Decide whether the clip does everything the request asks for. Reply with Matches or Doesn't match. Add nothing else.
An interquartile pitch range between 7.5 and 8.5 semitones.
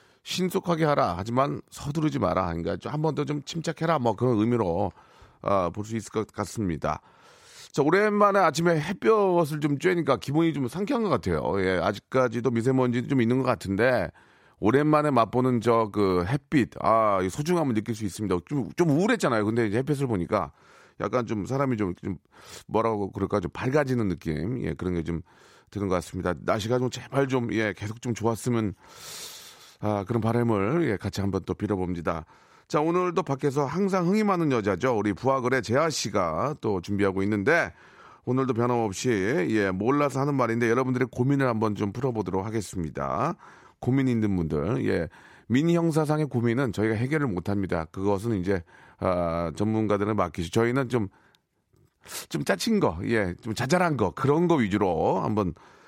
Doesn't match